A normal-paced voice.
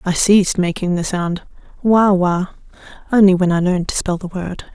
Yes: average, 190 wpm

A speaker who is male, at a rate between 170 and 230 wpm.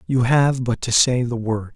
No: male; fast, 240 wpm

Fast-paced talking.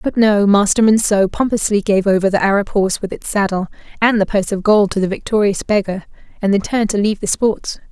Yes: fast, 210 wpm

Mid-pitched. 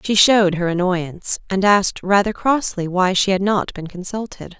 No: high, 195 Hz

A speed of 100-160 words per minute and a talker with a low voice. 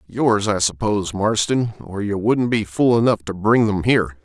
No: average, 200 wpm; low, 105 Hz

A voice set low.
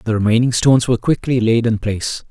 Yes: low, 115 Hz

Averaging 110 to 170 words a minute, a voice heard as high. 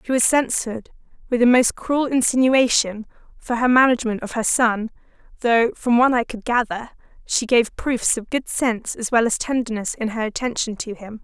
No: average, 185 wpm; high, 235 Hz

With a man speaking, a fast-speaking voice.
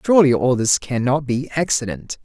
No: male; average, 160 wpm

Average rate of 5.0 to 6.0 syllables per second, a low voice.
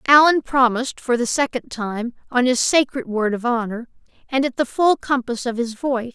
No: 5.1 syllables/s; very high, 250 Hz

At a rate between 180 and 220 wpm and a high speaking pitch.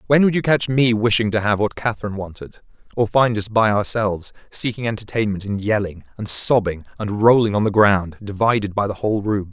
No: average, 200 wpm; low, 105 Hz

